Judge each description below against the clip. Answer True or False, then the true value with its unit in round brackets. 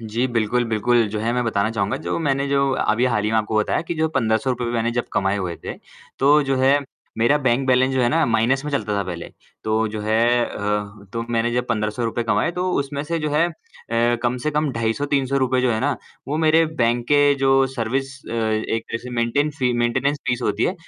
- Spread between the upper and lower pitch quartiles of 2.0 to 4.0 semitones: True (3.6 semitones)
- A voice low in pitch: True (120 Hz)